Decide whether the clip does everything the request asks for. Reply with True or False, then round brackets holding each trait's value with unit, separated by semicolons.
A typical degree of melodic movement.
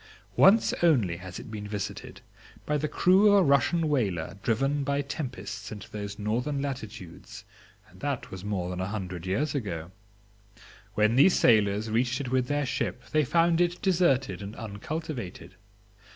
False (6.4 semitones)